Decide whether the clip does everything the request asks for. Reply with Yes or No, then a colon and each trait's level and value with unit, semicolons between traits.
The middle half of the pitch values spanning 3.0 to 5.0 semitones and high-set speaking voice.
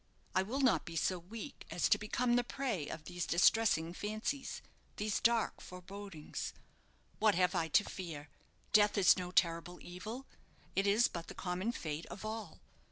Yes: average, 4.1 semitones; high, 195 Hz